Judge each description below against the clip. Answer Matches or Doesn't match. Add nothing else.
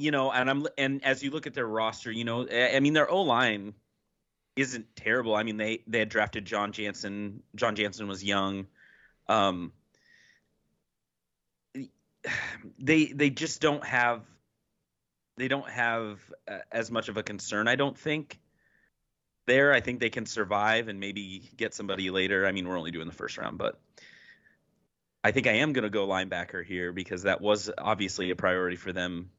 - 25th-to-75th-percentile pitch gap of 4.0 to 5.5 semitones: Matches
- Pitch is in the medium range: Doesn't match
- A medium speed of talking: Matches